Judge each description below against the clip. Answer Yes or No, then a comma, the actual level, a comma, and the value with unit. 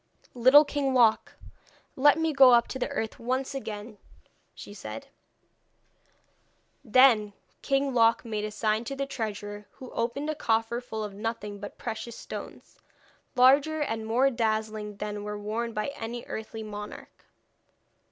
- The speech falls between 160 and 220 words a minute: No, average, 145 wpm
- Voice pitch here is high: Yes, high, 230 Hz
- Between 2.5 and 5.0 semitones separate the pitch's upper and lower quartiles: Yes, average, 3.6 semitones